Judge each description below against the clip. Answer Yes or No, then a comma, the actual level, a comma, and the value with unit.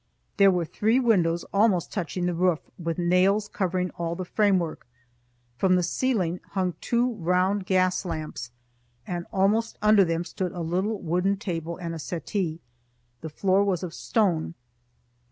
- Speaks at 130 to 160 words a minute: Yes, average, 155 wpm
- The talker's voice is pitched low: No, medium, 180 Hz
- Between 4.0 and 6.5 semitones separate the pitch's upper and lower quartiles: No, average, 2.8 semitones